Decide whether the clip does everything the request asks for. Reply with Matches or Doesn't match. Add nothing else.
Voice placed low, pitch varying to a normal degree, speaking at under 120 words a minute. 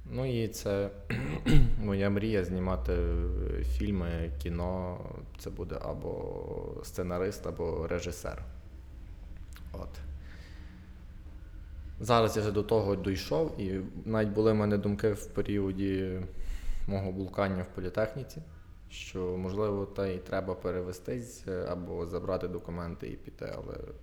Matches